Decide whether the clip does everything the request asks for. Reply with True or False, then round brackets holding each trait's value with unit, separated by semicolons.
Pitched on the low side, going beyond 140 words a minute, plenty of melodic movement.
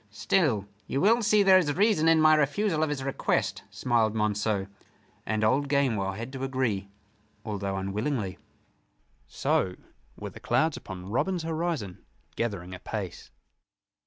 False (125 Hz; 135 wpm; 7.5 semitones)